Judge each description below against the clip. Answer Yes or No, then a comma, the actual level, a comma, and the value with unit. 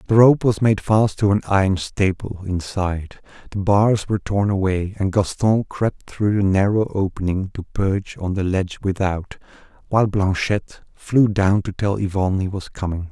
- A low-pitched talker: Yes, low, 100 Hz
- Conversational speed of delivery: Yes, average, 175 wpm